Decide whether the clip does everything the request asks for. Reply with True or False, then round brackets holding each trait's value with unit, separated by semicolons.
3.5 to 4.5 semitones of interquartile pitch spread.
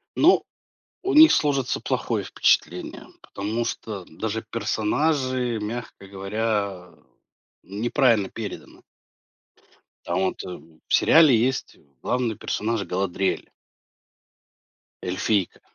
True (4.2 semitones)